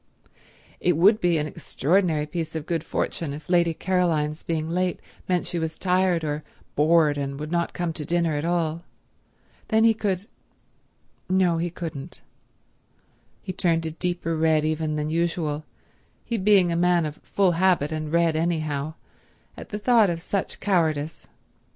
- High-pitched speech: No, medium, 165 Hz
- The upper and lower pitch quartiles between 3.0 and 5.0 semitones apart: No, narrow, 2.5 semitones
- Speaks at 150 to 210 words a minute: Yes, average, 155 wpm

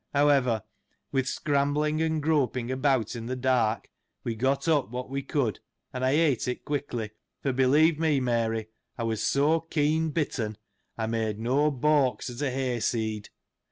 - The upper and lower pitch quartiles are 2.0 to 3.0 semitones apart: No, average, 3.9 semitones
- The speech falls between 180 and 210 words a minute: No, average, 165 wpm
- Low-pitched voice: Yes, low, 130 Hz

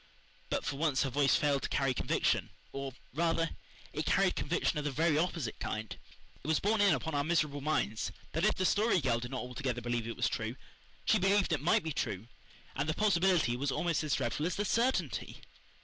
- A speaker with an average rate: No, fast, 210 wpm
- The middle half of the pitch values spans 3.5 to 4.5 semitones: No, average, 4.9 semitones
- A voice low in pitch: No, medium, 150 Hz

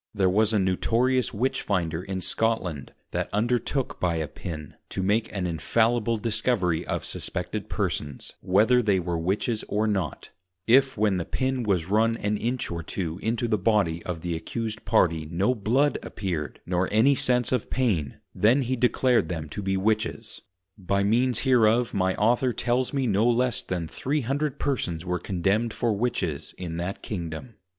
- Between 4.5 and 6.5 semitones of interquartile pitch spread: Yes, average, 5.0 semitones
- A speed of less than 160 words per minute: No, average, 165 wpm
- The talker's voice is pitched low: Yes, low, 105 Hz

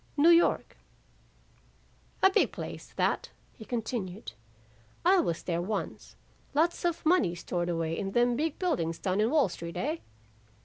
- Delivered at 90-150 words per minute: Yes, average, 145 wpm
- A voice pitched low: No, high, 225 Hz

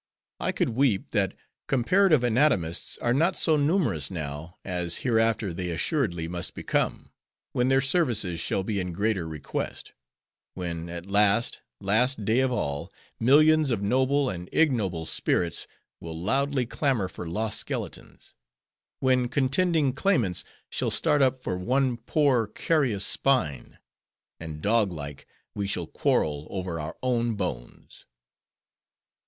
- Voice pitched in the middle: No, low, 110 Hz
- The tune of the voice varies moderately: No, wide, 7.2 semitones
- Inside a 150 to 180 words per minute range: No, slow, 135 wpm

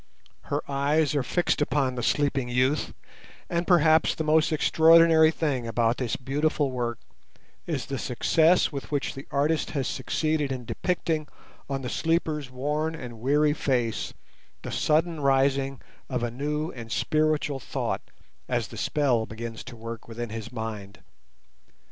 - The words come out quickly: No, average, 150 wpm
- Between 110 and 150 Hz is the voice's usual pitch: Yes, medium, 140 Hz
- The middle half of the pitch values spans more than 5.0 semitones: No, average, 4.0 semitones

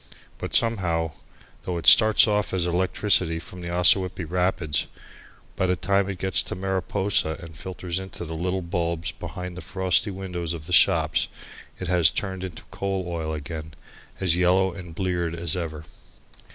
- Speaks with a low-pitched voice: Yes, very low, 90 Hz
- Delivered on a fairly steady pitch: Yes, narrow, 2.1 semitones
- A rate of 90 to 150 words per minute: No, average, 165 wpm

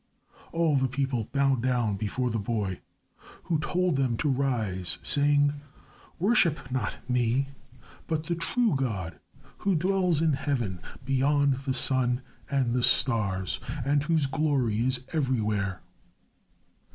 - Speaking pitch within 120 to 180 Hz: Yes, low, 135 Hz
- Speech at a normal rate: No, slow, 130 wpm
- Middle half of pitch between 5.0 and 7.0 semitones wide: No, average, 4.1 semitones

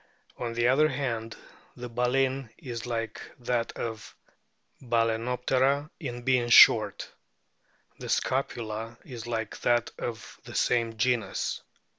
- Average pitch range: No, narrow, 1.9 semitones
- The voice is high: No, low, 120 Hz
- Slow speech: Yes, slow, 115 wpm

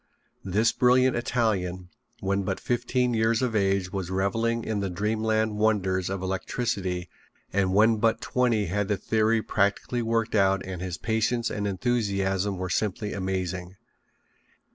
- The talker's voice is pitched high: No, low, 105 Hz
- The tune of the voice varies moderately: Yes, average, 3.1 semitones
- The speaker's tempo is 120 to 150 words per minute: Yes, average, 140 wpm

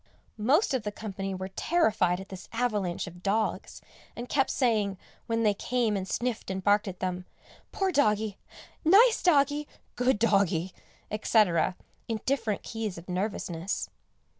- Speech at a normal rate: Yes, average, 145 wpm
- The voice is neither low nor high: No, high, 210 Hz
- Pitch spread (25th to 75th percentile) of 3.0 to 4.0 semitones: No, average, 4.6 semitones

